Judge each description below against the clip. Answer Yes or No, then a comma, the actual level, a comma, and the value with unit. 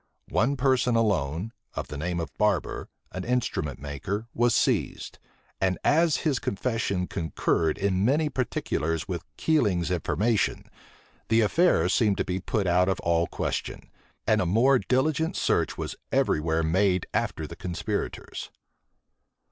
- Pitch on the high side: No, low, 100 Hz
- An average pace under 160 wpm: Yes, average, 140 wpm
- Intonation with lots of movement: Yes, wide, 6.0 semitones